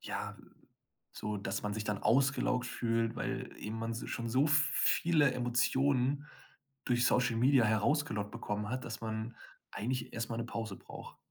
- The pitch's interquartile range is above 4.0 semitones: No, average, 2.9 semitones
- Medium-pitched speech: No, low, 115 Hz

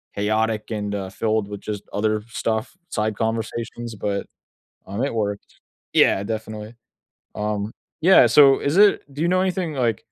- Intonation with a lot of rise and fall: No, narrow, 2.6 semitones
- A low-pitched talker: Yes, low, 110 Hz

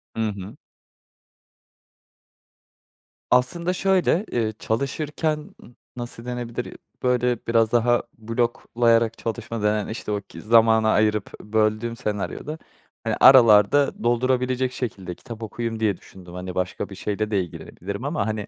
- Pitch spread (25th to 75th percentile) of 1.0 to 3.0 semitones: Yes, average, 2.7 semitones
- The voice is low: Yes, low, 115 Hz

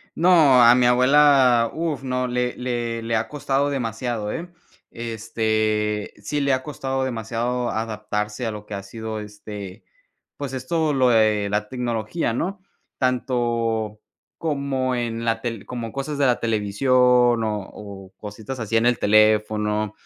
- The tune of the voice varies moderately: Yes, average, 3.2 semitones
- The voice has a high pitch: No, low, 115 Hz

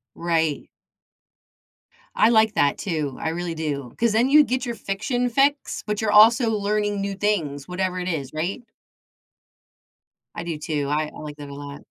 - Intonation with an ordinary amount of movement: No, wide, 6.3 semitones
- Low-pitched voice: No, medium, 185 Hz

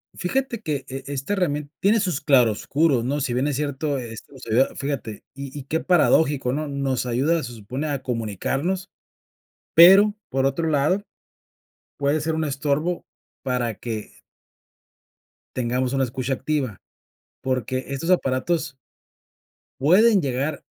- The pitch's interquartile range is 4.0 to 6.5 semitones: No, average, 3.6 semitones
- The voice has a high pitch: No, medium, 140 Hz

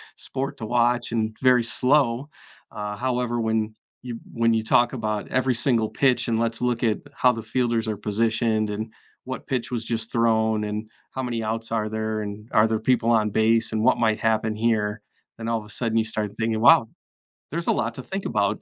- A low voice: Yes, low, 115 Hz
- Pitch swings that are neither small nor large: No, narrow, 1.7 semitones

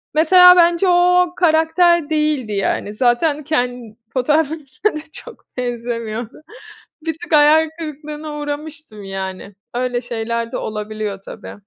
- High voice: Yes, very high, 295 Hz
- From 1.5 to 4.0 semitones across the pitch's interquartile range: No, wide, 5.6 semitones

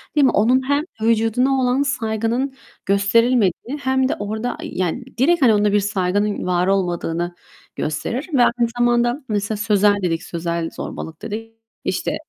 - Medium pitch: No, high, 220 Hz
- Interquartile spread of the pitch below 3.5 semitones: No, average, 4.2 semitones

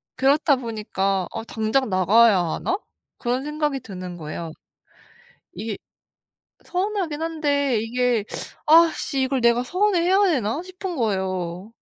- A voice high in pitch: Yes, very high, 250 Hz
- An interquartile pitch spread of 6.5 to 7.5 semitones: Yes, wide, 6.9 semitones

